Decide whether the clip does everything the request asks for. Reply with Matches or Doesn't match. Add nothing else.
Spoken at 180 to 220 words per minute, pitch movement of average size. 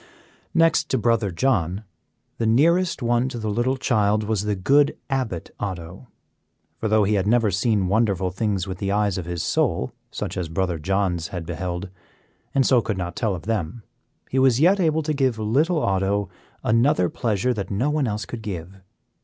Matches